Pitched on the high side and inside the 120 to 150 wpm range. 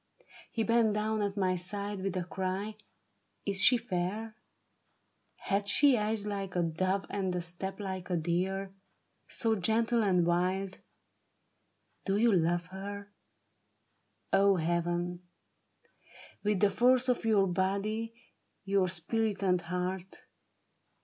Yes: high, 195 Hz; slow, 135 wpm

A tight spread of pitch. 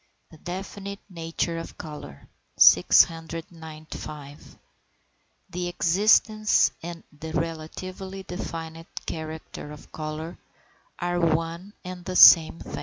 Yes: narrow, 2.2 semitones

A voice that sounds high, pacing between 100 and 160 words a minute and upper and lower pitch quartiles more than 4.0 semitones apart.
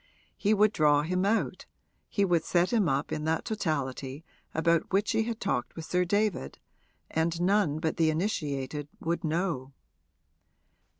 No: medium, 165 Hz; average, 155 wpm; average, 4.6 semitones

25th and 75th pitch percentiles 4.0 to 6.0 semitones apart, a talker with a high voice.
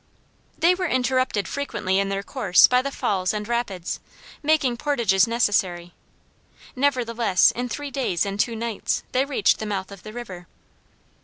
Yes: average, 4.8 semitones; high, 230 Hz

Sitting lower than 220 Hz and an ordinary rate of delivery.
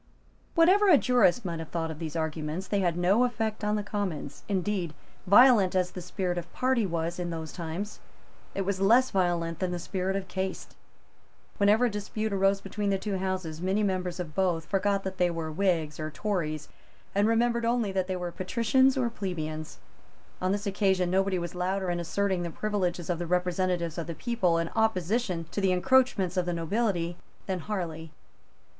Yes: medium, 185 Hz; average, 190 wpm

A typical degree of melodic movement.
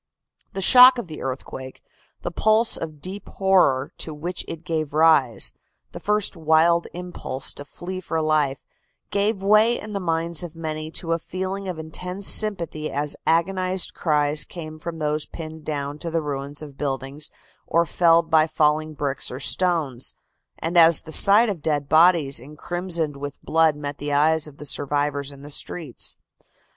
Yes: average, 3.3 semitones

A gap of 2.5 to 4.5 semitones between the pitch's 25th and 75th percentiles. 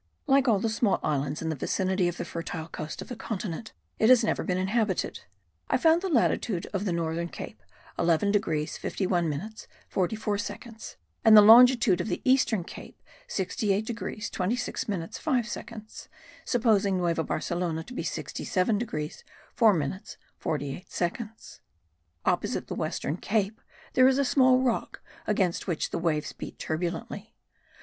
No: average, 5.0 semitones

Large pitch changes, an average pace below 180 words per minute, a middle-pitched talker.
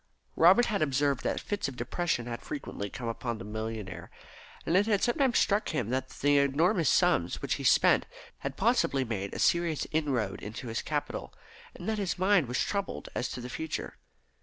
No: wide, 7.3 semitones; average, 185 wpm; medium, 145 Hz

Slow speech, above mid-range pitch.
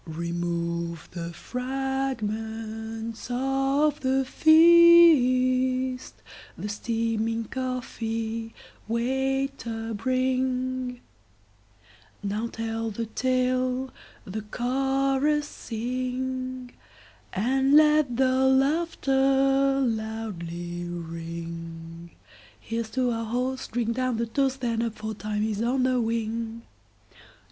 Yes: slow, 80 wpm; high, 240 Hz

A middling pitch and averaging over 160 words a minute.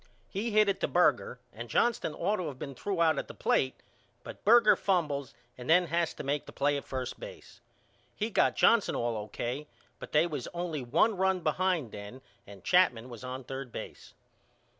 Yes: medium, 150 Hz; average, 195 wpm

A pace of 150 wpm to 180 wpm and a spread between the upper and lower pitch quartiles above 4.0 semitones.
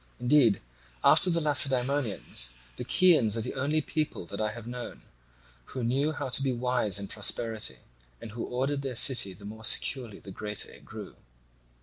Yes: average, 175 wpm; average, 4.4 semitones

